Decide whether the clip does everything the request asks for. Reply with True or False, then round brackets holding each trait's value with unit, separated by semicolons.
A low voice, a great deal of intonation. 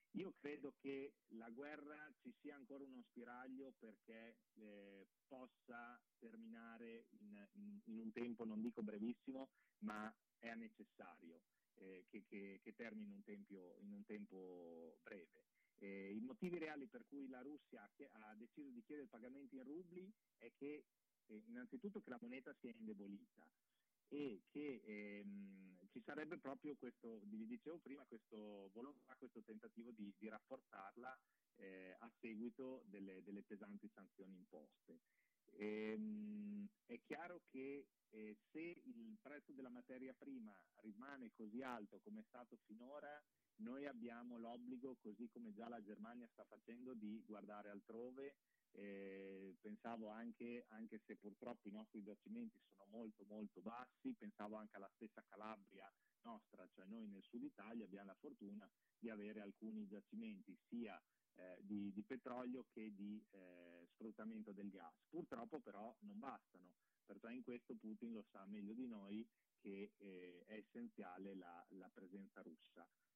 True (115 Hz; 5.7 semitones)